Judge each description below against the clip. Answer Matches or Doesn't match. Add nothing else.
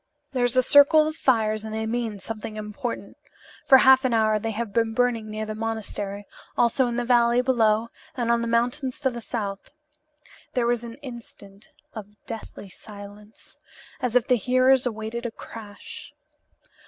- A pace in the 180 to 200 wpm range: Doesn't match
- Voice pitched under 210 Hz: Doesn't match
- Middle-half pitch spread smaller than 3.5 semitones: Matches